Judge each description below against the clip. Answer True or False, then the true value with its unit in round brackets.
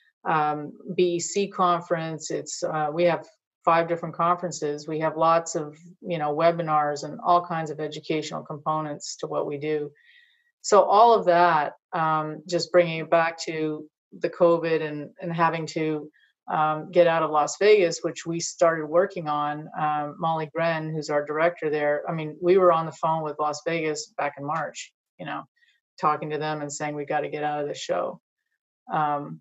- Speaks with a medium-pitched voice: True (160 Hz)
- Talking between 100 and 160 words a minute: False (185 wpm)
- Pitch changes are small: True (2.2 semitones)